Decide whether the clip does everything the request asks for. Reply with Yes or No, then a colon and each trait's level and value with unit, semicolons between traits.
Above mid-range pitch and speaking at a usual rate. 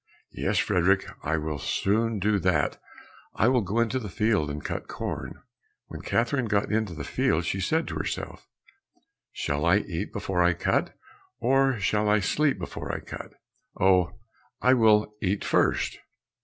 No: low, 105 Hz; average, 160 wpm